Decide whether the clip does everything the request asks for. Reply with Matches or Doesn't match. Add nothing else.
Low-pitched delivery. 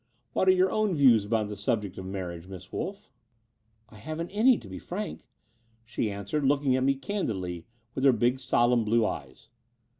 Matches